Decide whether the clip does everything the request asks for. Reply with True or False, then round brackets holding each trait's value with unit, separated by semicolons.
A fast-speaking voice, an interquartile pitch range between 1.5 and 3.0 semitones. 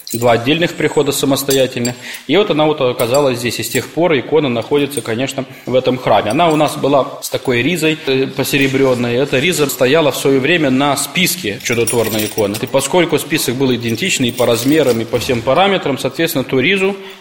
False (185 wpm; 3.6 semitones)